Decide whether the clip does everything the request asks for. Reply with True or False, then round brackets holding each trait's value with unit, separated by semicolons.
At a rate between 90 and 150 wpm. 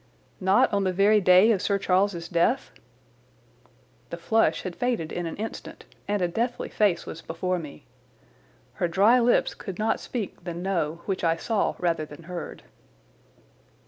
False (160 wpm)